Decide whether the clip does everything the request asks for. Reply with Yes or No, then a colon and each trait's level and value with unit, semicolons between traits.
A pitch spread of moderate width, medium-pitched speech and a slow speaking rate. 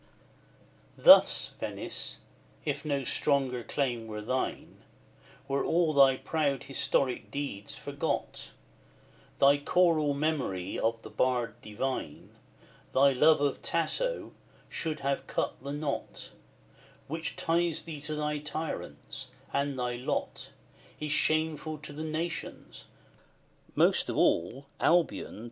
Yes: average, 3.1 semitones; medium, 145 Hz; slow, 120 wpm